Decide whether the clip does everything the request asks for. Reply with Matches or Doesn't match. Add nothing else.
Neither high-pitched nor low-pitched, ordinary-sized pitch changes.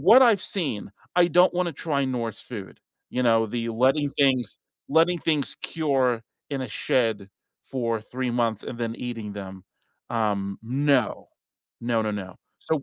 Doesn't match